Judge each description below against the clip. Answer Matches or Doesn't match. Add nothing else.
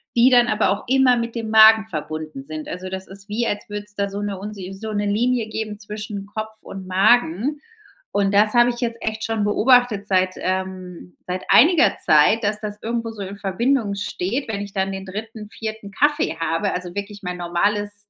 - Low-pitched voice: Doesn't match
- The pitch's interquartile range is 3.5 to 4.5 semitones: Doesn't match